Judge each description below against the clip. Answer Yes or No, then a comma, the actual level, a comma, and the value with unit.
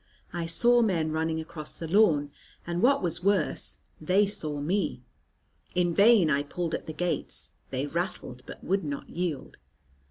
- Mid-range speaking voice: Yes, medium, 170 Hz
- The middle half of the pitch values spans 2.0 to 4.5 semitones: Yes, average, 3.9 semitones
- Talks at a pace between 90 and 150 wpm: No, average, 160 wpm